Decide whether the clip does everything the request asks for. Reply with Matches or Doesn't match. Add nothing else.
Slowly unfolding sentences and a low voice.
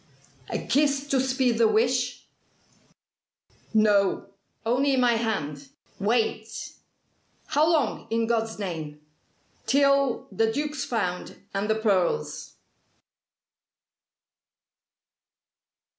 Doesn't match